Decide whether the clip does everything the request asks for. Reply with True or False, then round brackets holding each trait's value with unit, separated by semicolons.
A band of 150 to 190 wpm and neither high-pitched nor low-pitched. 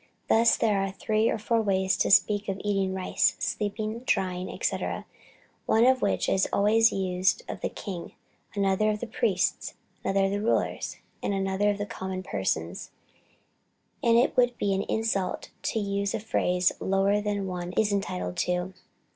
False (160 wpm; 200 Hz)